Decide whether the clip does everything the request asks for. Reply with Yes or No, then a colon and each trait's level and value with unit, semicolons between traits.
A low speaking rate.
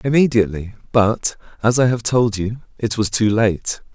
No: average, 165 wpm